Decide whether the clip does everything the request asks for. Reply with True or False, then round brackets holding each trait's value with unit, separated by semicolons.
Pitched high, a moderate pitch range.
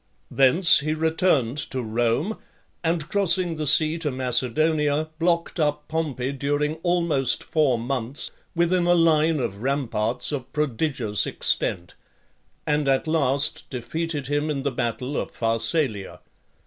False (145 Hz; 4.1 semitones)